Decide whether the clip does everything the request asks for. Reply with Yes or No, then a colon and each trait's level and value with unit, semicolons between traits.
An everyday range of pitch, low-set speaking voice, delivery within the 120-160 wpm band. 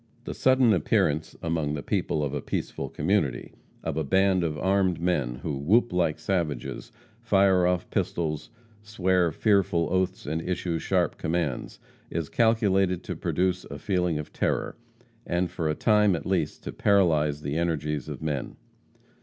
Yes: average, 3.9 semitones; very low, 85 Hz; average, 155 wpm